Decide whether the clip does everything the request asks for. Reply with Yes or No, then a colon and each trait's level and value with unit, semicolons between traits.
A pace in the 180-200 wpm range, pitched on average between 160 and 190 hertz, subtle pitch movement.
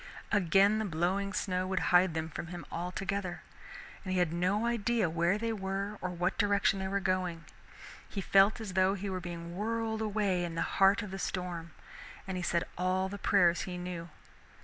Yes: average, 190 wpm; medium, 185 Hz; narrow, 2.2 semitones